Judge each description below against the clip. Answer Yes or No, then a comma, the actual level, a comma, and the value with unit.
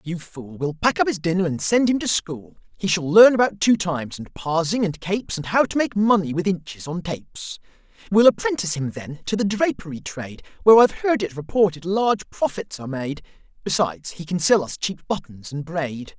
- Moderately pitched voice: Yes, medium, 180 Hz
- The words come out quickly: Yes, fast, 210 wpm